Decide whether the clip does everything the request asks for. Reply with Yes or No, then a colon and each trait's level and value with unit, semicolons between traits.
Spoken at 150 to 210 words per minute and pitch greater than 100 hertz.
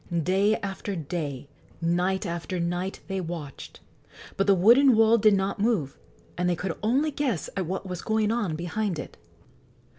Yes: average, 160 wpm; high, 190 Hz